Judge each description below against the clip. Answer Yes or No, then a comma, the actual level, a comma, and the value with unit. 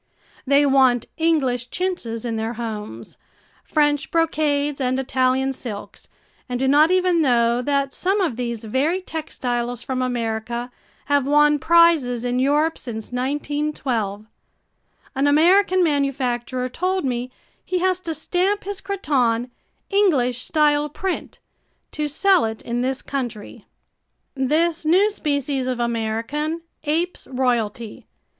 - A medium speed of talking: No, slow, 125 wpm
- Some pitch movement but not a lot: Yes, average, 4.6 semitones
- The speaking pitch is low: No, very high, 275 Hz